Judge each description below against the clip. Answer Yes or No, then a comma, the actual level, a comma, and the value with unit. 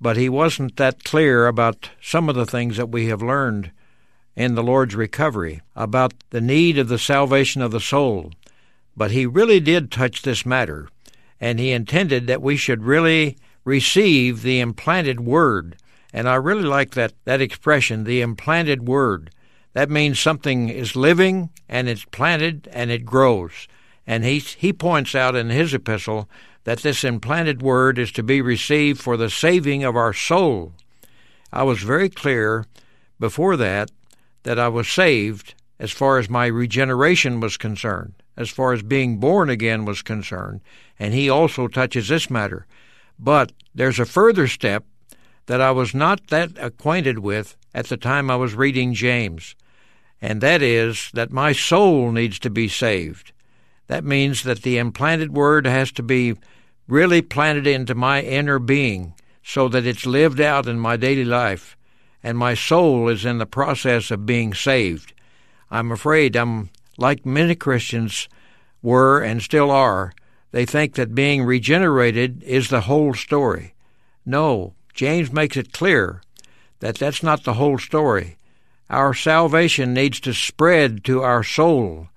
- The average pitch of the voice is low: Yes, low, 125 Hz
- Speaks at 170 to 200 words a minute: No, average, 160 wpm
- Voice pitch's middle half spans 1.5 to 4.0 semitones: Yes, average, 3.4 semitones